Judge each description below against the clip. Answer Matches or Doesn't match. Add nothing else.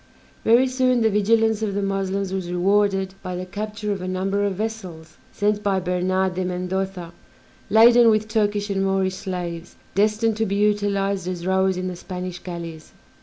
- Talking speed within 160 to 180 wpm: Matches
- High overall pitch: Matches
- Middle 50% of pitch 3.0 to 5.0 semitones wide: Doesn't match